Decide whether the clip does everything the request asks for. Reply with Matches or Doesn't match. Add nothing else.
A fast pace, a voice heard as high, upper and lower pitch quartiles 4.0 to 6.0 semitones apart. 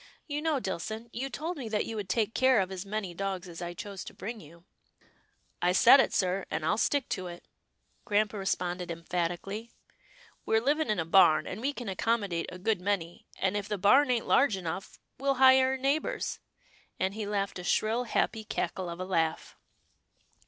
Matches